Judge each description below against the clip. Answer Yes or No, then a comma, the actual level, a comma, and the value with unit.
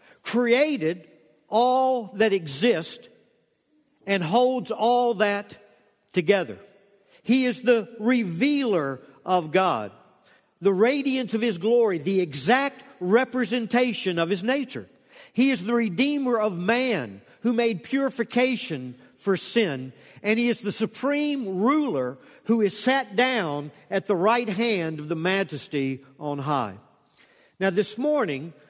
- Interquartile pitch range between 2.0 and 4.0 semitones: No, wide, 5.4 semitones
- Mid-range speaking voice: No, high, 220 Hz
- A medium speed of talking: No, slow, 125 wpm